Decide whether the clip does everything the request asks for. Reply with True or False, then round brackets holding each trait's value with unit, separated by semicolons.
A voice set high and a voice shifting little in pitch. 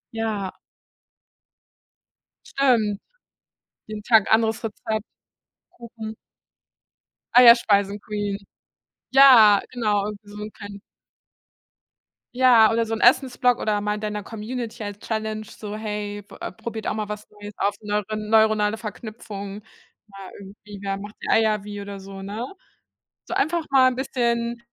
True (215 Hz; 2.1 semitones)